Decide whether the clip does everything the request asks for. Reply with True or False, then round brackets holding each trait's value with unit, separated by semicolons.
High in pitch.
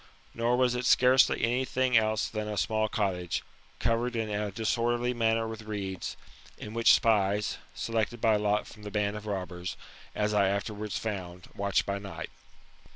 False (110 Hz)